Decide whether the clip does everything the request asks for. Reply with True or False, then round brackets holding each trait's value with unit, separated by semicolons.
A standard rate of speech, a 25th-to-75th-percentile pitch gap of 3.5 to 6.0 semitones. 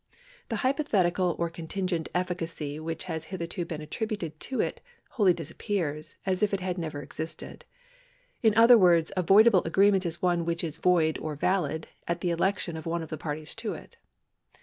False (175 wpm; 3.1 semitones)